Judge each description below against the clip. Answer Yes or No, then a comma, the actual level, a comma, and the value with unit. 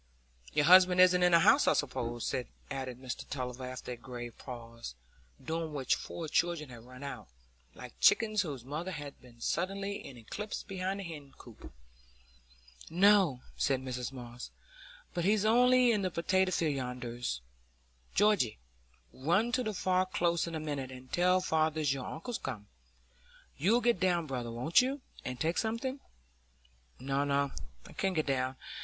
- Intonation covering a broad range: Yes, wide, 6.5 semitones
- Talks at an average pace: Yes, average, 160 wpm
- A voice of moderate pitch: Yes, medium, 155 Hz